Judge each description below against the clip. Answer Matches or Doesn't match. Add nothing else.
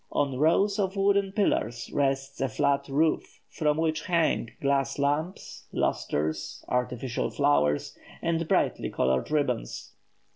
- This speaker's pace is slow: Matches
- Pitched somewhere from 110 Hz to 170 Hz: Matches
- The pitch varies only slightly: Doesn't match